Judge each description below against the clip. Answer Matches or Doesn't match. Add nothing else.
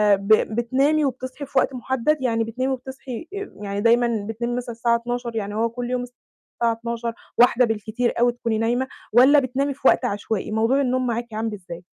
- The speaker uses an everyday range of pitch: Doesn't match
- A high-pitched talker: Matches